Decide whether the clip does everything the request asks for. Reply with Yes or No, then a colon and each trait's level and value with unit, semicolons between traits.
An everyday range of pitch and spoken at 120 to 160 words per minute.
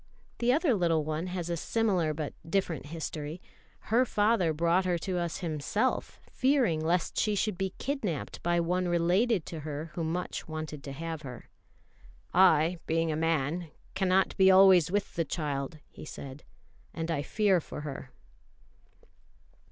Yes: average, 3.4 semitones; average, 155 wpm